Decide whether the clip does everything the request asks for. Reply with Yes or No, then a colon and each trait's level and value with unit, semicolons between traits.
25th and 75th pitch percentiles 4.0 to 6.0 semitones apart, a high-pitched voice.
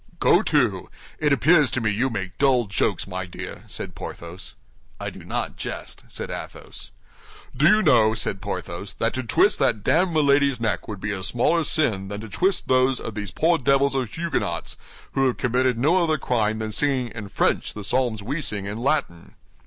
No: average, 5.2 semitones; low, 125 Hz